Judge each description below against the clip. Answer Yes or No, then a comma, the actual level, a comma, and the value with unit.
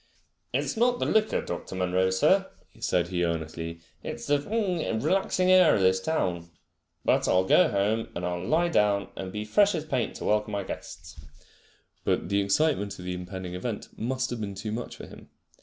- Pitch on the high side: No, low, 105 Hz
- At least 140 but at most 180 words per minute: No, average, 190 wpm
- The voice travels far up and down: Yes, wide, 7.9 semitones